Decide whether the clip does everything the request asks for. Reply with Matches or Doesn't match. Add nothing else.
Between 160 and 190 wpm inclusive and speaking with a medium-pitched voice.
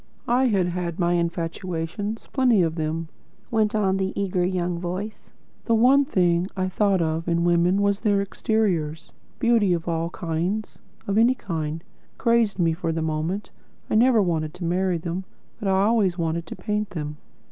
Matches